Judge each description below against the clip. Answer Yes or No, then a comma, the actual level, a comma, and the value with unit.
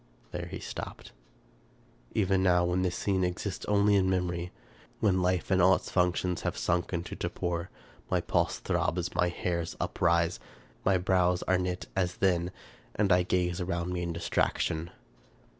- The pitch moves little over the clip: Yes, narrow, 1.2 semitones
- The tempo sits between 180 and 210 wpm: No, average, 160 wpm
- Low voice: Yes, very low, 90 Hz